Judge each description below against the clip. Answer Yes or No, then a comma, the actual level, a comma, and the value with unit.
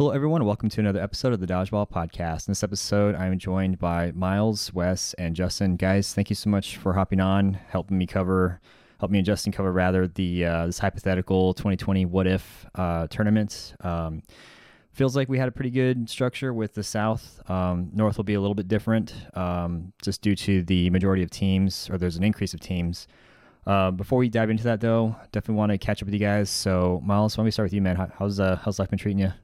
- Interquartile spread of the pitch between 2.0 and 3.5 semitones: Yes, narrow, 2.4 semitones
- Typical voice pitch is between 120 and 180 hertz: No, low, 100 Hz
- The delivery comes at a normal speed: No, fast, 230 wpm